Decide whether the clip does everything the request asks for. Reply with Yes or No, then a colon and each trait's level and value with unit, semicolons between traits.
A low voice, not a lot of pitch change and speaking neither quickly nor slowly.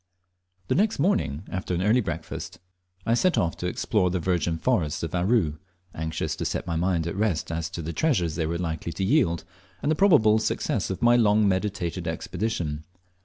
No: very low, 90 Hz; average, 4.9 semitones; average, 190 wpm